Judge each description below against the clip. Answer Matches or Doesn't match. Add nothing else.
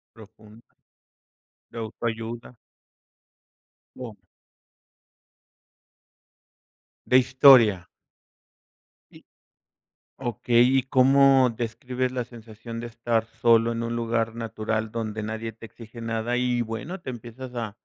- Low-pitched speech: Matches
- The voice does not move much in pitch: Matches